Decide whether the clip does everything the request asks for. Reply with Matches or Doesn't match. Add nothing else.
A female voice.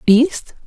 Matches